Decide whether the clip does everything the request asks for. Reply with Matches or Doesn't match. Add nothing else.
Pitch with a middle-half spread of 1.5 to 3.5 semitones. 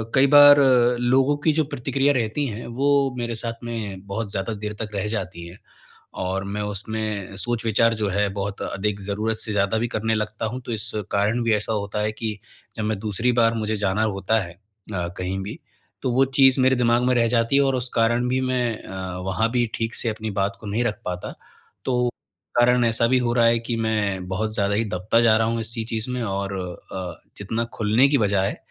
Matches